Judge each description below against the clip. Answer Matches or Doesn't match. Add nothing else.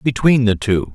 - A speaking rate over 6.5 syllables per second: Doesn't match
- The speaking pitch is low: Matches